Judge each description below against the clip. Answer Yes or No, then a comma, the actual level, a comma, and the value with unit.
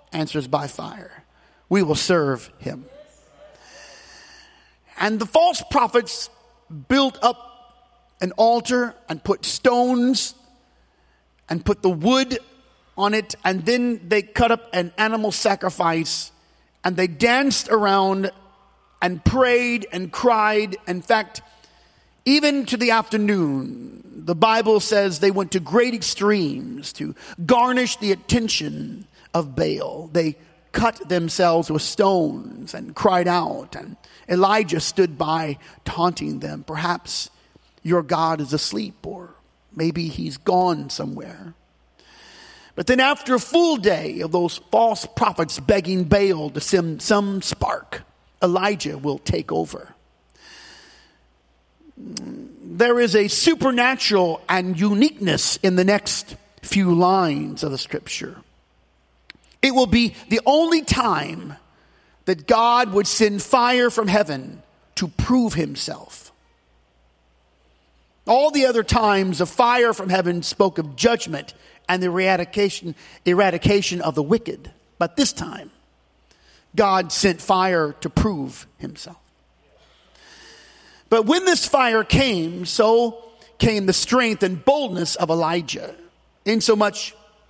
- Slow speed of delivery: Yes, slow, 120 wpm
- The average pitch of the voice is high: Yes, high, 200 Hz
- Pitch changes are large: Yes, wide, 5.7 semitones